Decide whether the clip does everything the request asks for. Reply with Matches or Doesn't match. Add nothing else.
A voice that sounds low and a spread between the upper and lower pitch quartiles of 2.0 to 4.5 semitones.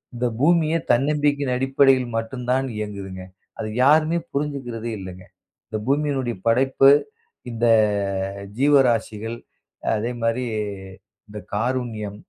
Matches